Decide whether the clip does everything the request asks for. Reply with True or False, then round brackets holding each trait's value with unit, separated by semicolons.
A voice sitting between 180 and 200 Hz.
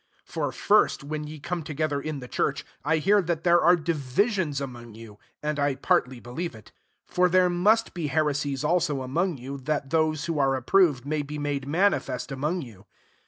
False (150 Hz)